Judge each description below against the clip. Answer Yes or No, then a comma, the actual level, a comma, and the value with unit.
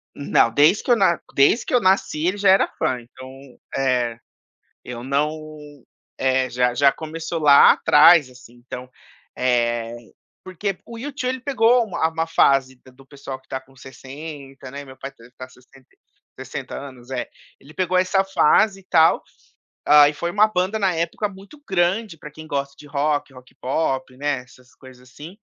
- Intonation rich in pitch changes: Yes, wide, 5.9 semitones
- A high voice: No, medium, 145 Hz